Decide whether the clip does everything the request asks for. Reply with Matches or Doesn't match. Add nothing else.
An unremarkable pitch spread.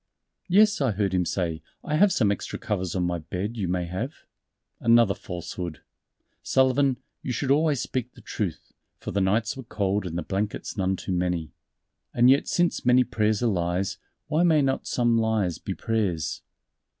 Doesn't match